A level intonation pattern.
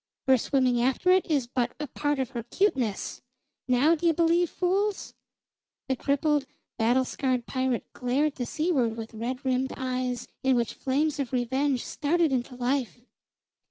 No: average, 3.3 semitones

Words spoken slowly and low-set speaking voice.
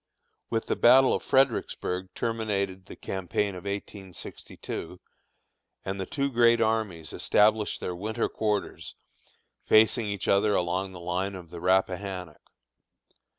Yes: slow, 125 wpm; low, 100 Hz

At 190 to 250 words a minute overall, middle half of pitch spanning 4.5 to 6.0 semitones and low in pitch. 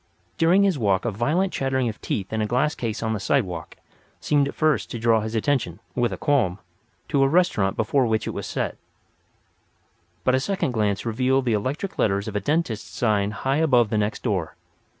Yes: average, 200 wpm; average, 4.9 semitones; low, 120 Hz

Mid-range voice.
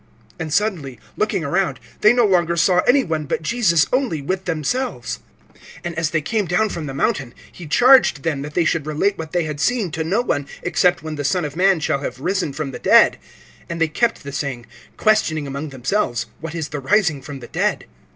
Yes: medium, 165 Hz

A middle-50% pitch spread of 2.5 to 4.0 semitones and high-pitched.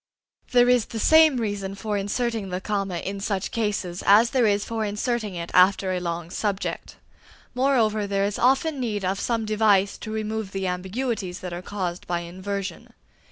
Yes: average, 3.1 semitones; high, 205 Hz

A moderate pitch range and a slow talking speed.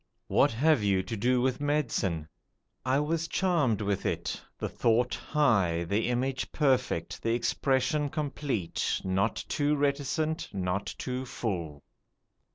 No: wide, 6.4 semitones; slow, 130 wpm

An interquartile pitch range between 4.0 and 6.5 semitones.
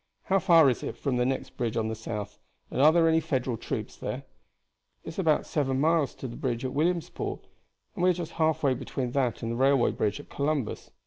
Yes: average, 4.8 semitones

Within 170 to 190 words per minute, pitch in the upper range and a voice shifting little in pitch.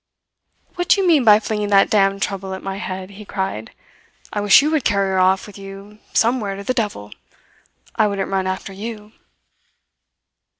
Yes: average, 185 wpm; high, 200 Hz; narrow, 1.9 semitones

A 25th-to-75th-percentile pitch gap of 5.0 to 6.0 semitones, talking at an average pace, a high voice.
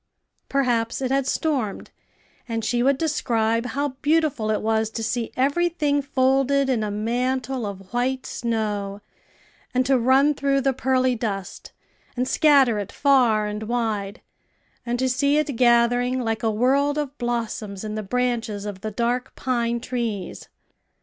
No: average, 3.4 semitones; average, 155 wpm; high, 245 Hz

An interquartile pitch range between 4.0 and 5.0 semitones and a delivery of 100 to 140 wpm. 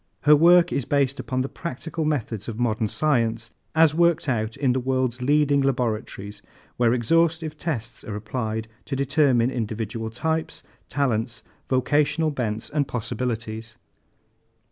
Yes: average, 4.7 semitones; slow, 135 wpm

